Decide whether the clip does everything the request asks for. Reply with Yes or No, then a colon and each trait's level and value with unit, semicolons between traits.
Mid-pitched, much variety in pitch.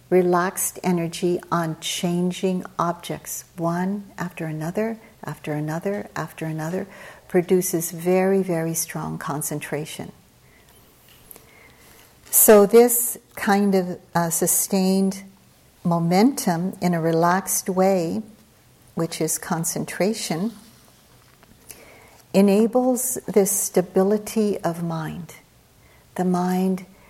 No: medium, 180 Hz; average, 2.9 semitones